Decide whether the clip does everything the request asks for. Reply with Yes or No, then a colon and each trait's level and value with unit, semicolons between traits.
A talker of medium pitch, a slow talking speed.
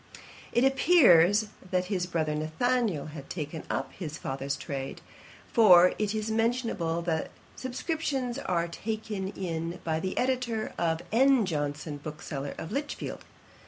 Yes: medium, 180 Hz; slow, 130 wpm